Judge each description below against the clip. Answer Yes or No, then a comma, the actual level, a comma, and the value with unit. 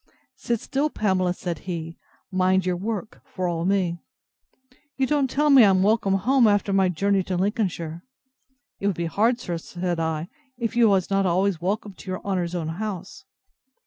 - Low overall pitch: No, high, 190 Hz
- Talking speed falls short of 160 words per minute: No, average, 175 wpm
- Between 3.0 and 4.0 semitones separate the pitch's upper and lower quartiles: Yes, average, 3.5 semitones